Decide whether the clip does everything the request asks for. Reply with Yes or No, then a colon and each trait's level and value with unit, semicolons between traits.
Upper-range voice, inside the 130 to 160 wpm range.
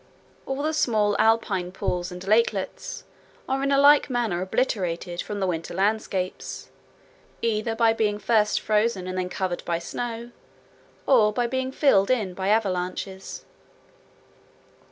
Yes: high, 210 Hz; slow, 135 wpm